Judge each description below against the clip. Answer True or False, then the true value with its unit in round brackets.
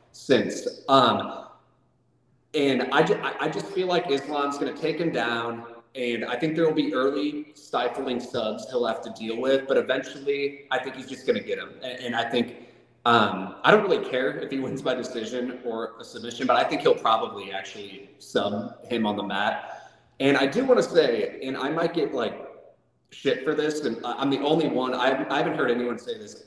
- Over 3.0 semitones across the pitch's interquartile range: True (4.3 semitones)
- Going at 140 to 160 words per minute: False (205 wpm)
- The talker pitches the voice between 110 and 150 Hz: True (135 Hz)